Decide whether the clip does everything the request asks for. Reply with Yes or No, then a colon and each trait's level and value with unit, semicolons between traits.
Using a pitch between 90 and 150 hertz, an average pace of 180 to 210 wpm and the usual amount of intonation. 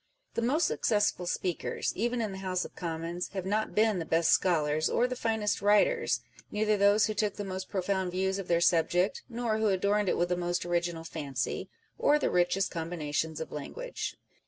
No: high, 190 Hz; average, 195 wpm; average, 3.6 semitones